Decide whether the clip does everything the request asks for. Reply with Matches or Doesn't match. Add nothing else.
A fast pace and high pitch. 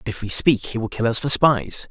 Doesn't match